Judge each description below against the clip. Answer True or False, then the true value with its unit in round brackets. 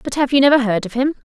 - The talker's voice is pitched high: True (255 Hz)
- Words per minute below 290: False (320 wpm)